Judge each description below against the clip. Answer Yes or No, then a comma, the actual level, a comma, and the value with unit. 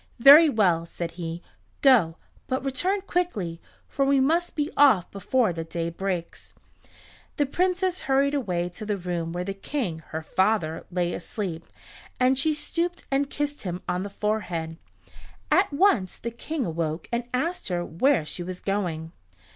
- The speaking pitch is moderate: No, high, 205 Hz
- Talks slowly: No, average, 160 wpm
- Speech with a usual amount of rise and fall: No, wide, 8.4 semitones